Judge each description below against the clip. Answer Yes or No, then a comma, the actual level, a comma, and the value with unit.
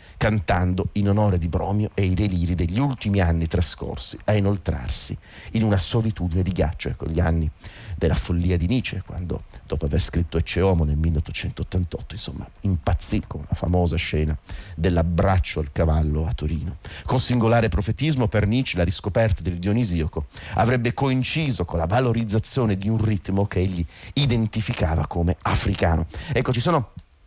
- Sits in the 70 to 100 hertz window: Yes, very low, 95 Hz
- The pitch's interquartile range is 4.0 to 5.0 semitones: Yes, average, 4.3 semitones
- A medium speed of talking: Yes, average, 150 wpm